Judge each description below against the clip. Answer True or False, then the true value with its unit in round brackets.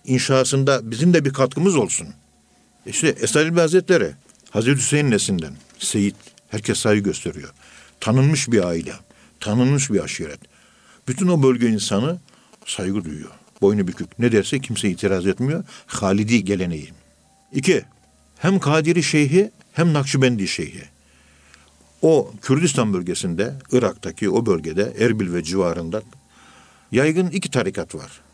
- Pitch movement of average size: False (7.4 semitones)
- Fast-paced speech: False (120 wpm)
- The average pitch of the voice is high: False (115 Hz)